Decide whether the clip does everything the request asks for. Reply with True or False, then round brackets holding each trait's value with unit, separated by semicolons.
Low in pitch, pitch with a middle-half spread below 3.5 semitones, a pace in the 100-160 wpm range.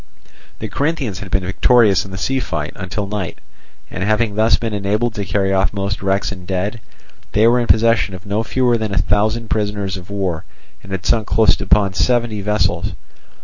False (105 Hz; 2.7 semitones; 190 wpm)